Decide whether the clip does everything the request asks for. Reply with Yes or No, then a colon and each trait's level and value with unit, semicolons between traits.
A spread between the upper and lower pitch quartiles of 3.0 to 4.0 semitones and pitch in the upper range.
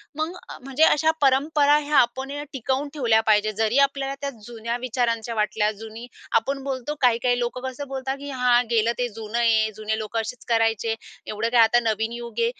Yes: average, 3.4 semitones; high, 240 Hz